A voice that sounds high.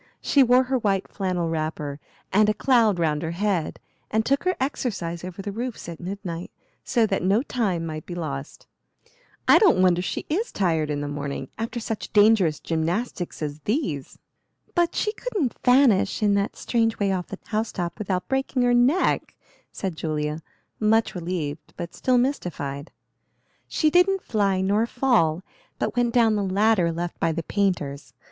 Yes: high, 195 Hz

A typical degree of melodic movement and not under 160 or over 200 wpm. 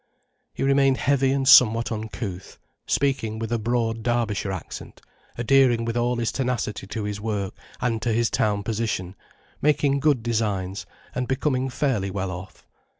No: average, 3.8 semitones; average, 150 wpm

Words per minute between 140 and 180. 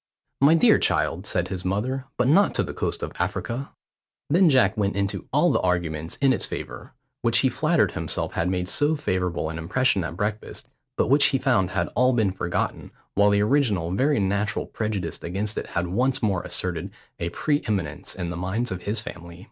No: average, 195 wpm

